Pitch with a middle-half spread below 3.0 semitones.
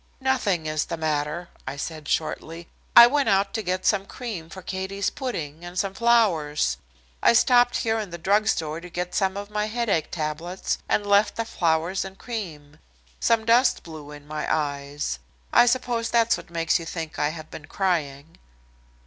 No: wide, 5.5 semitones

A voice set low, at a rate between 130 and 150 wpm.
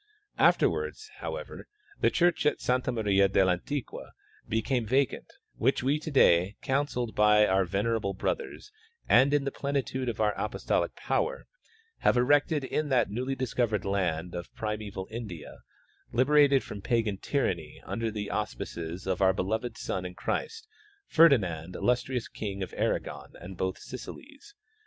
Yes: low, 115 Hz; average, 140 wpm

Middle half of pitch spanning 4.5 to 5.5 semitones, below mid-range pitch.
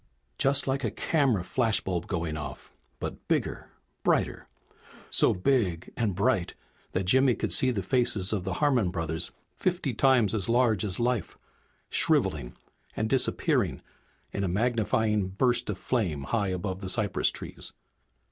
Yes: average, 5.2 semitones; low, 105 Hz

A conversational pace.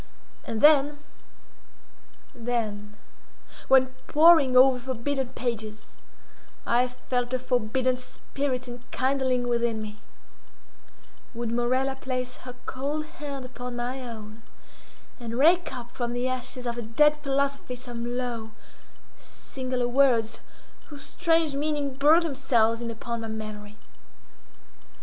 No: slow, 110 wpm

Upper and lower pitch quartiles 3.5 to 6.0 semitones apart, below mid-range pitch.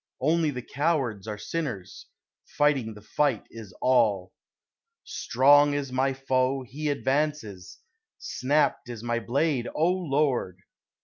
Yes: average, 4.1 semitones; low, 130 Hz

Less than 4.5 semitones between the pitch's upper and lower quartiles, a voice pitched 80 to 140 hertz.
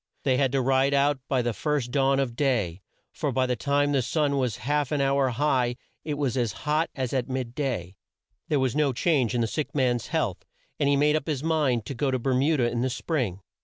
Yes: average, 2.8 semitones; low, 135 Hz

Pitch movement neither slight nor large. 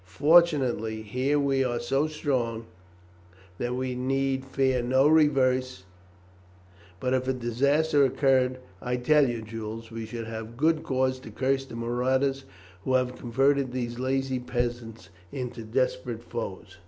No: narrow, 2.2 semitones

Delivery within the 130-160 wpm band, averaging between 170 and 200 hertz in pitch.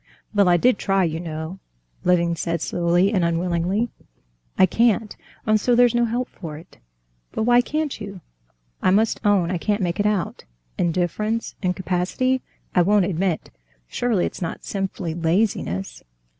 Yes: average, 150 wpm; high, 190 Hz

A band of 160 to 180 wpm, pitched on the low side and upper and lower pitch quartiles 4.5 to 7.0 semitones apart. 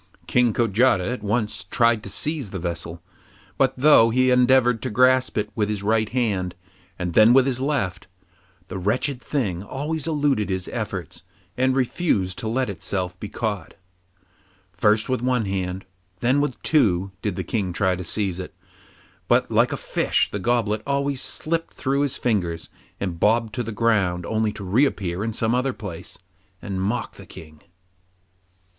Yes: average, 170 wpm; low, 110 Hz; average, 5.0 semitones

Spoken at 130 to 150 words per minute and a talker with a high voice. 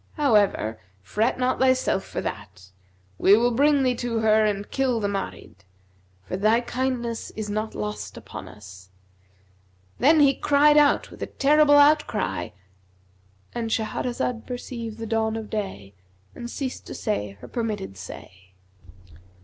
Yes: average, 140 wpm; high, 220 Hz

